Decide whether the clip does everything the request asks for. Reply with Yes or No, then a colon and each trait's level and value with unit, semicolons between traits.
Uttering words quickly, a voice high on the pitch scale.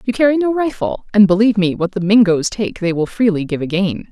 Yes: fast, 235 wpm; high, 200 Hz